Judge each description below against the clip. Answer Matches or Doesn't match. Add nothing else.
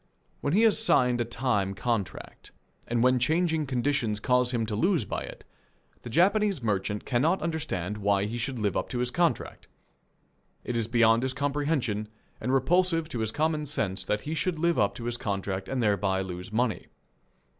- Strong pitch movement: Matches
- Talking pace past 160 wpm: Matches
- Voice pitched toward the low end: Matches